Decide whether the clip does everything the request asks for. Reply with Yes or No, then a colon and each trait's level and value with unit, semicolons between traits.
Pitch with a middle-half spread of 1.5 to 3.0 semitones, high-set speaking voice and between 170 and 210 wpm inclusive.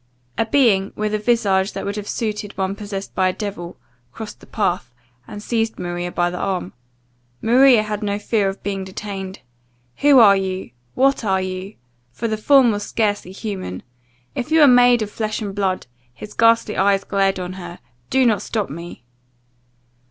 Yes: average, 2.7 semitones; high, 205 Hz; average, 180 wpm